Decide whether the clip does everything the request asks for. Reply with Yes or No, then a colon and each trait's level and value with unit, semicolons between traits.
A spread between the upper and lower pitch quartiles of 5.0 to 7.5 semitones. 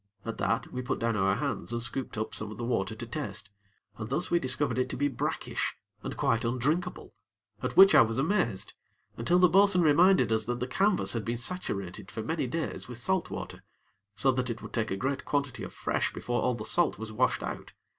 Yes: average, 5.3 semitones